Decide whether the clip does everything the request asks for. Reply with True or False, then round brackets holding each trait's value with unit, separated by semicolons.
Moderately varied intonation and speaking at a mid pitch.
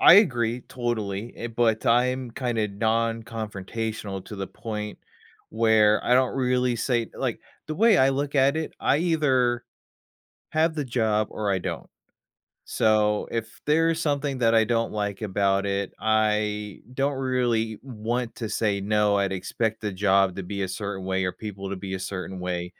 False (3.7 semitones; 110 Hz)